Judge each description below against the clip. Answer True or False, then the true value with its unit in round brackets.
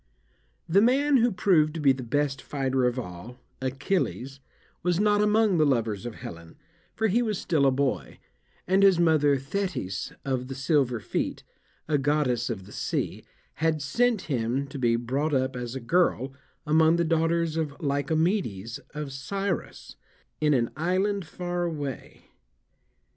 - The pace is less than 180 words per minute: True (155 wpm)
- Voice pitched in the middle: True (145 Hz)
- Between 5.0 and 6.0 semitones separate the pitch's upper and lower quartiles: True (5.3 semitones)